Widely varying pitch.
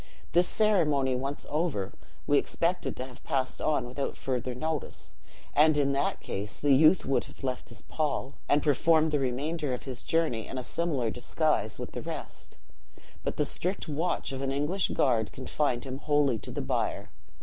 No: average, 3.4 semitones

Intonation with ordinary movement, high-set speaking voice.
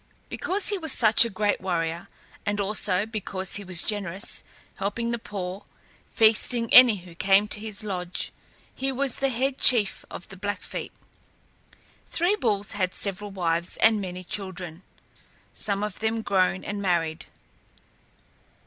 Yes: average, 3.3 semitones; high, 205 Hz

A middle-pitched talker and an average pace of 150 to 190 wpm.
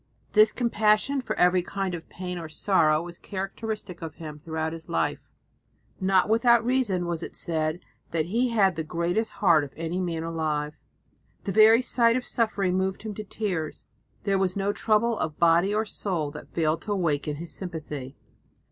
Yes: medium, 180 Hz; average, 175 wpm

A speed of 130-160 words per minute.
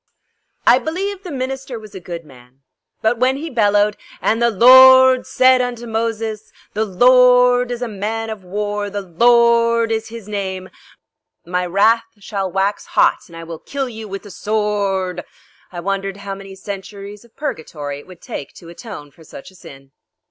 No: average, 175 wpm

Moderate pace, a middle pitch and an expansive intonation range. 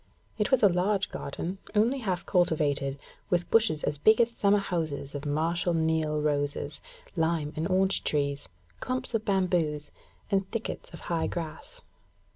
No: average, 150 wpm; medium, 175 Hz; average, 4.6 semitones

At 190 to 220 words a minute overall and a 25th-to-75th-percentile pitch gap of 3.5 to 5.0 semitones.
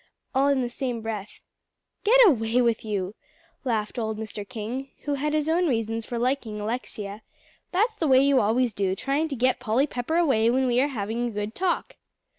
Yes: average, 195 wpm; average, 4.1 semitones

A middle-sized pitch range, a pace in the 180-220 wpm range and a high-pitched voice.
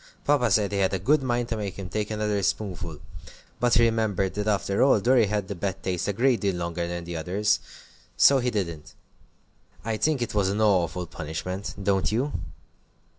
No: average, 3.6 semitones; average, 195 wpm; low, 100 Hz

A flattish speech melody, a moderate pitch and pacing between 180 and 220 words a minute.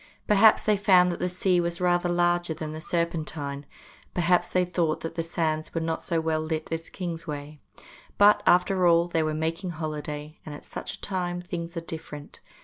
Yes: narrow, 2.1 semitones; medium, 170 Hz; average, 190 wpm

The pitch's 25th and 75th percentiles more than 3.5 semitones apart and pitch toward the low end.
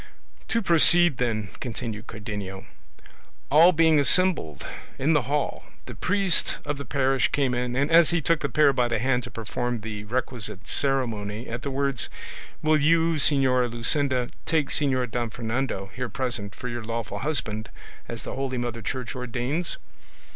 Yes: average, 3.9 semitones; low, 130 Hz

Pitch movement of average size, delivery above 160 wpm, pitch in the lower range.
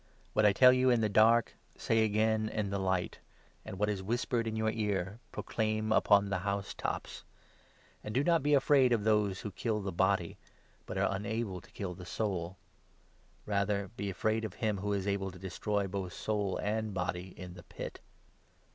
No: narrow, 2.3 semitones; average, 185 wpm; low, 105 Hz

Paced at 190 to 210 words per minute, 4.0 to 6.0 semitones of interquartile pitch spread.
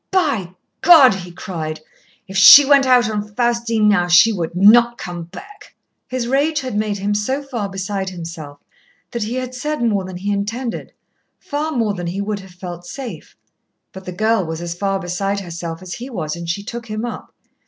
Yes: average, 195 wpm; average, 5.1 semitones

